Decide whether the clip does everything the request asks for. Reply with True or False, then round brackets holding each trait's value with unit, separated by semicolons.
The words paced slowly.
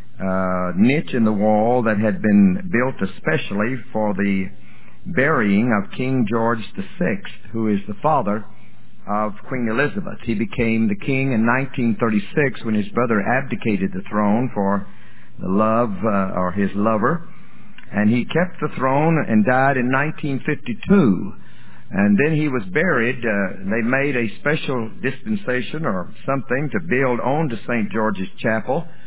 False (150 wpm)